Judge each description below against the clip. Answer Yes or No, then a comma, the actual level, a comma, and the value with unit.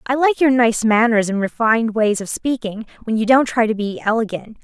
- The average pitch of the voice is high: Yes, high, 230 Hz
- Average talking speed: No, fast, 220 wpm